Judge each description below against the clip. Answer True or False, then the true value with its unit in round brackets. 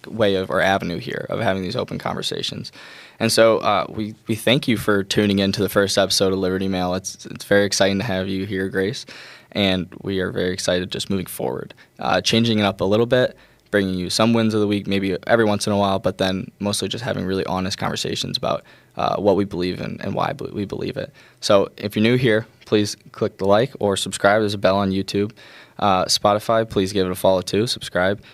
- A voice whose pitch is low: True (100 Hz)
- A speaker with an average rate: False (230 wpm)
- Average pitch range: False (2.1 semitones)